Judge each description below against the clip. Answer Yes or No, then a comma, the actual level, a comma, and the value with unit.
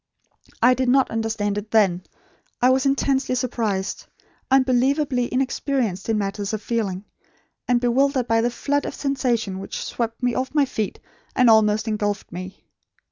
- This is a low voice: No, high, 235 Hz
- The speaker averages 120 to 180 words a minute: Yes, average, 150 wpm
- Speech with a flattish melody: No, average, 3.7 semitones